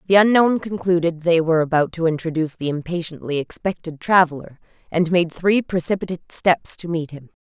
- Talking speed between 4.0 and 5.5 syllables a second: No, 5.7 syllables/s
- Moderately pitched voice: Yes, medium, 170 Hz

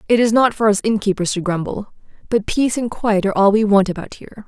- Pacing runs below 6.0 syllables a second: No, 6.4 syllables/s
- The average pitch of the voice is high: Yes, high, 210 Hz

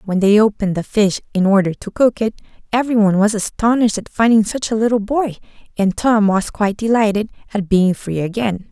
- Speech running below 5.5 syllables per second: No, 5.8 syllables/s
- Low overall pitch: No, high, 210 Hz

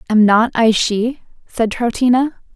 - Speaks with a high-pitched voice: Yes, high, 230 Hz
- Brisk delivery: No, average, 140 wpm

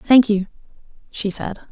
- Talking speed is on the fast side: No, average, 140 wpm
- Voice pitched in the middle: No, high, 215 Hz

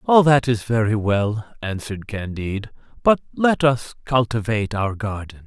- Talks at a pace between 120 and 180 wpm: Yes, average, 145 wpm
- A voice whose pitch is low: Yes, low, 115 Hz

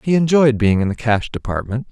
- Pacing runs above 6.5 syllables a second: No, 5.6 syllables/s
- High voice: No, low, 125 Hz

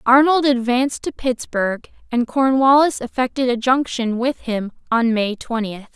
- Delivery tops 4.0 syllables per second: Yes, 4.7 syllables/s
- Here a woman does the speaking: Yes, female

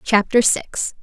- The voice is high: Yes, high, 220 Hz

